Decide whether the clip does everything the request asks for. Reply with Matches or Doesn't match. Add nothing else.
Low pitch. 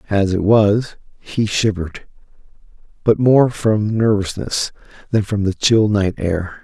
Matches